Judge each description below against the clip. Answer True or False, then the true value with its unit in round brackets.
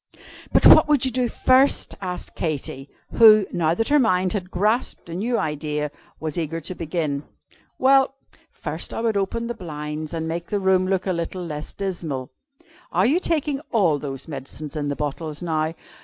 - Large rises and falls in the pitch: True (6.3 semitones)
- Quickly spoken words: False (180 wpm)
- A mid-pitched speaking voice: True (175 Hz)